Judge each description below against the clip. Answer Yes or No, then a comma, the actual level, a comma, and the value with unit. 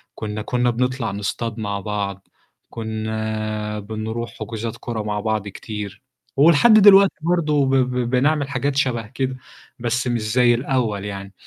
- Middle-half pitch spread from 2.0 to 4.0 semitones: Yes, average, 3.5 semitones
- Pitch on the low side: Yes, low, 115 Hz